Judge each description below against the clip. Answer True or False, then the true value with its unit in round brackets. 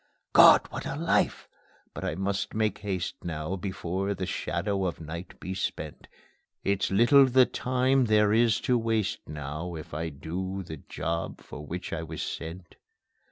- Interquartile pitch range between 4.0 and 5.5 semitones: True (4.4 semitones)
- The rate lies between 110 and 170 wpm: True (160 wpm)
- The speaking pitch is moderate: False (95 Hz)